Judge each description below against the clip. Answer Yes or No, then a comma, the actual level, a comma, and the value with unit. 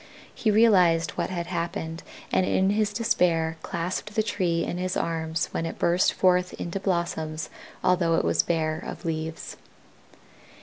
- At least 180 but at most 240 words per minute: No, average, 150 wpm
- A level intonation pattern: Yes, narrow, 2.2 semitones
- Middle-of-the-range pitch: Yes, medium, 170 Hz